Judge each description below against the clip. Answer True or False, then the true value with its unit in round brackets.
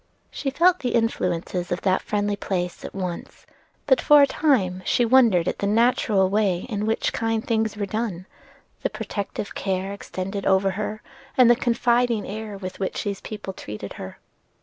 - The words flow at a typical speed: True (170 wpm)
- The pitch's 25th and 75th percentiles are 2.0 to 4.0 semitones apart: True (3.5 semitones)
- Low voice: False (205 Hz)